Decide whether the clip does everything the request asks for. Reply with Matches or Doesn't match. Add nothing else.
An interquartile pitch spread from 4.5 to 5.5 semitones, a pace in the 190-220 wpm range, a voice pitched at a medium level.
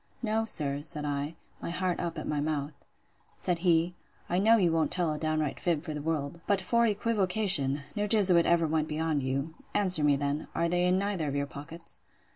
Doesn't match